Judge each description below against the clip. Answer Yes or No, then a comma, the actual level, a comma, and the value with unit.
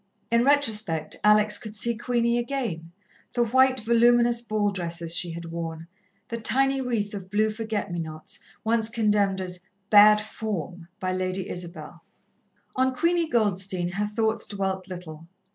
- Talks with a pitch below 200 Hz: No, high, 210 Hz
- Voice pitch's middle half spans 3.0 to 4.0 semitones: No, average, 4.6 semitones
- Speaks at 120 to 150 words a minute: Yes, average, 145 wpm